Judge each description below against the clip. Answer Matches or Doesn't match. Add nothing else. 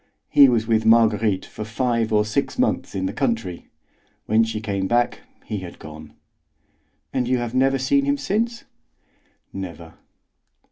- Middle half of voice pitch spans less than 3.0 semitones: Doesn't match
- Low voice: Matches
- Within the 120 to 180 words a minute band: Matches